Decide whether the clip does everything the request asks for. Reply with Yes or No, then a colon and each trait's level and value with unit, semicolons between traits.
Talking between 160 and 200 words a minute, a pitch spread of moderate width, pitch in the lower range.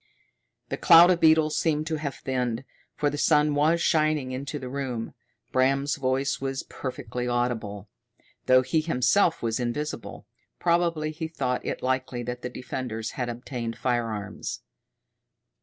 No: average, 140 wpm; average, 3.8 semitones; low, 130 Hz